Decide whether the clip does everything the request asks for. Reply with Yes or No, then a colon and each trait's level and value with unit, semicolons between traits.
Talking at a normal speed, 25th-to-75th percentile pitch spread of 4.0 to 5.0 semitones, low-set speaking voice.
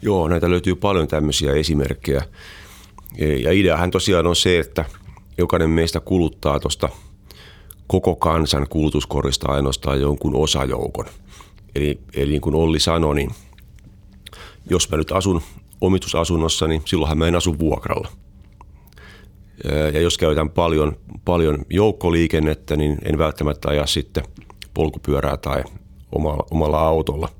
No: average, 120 wpm; average, 3.2 semitones; very low, 80 Hz